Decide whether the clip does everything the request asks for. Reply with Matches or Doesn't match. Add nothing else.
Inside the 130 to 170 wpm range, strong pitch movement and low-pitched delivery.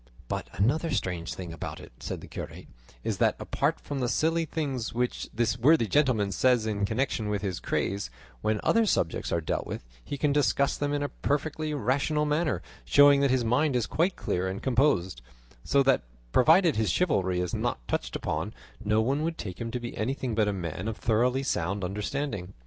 Doesn't match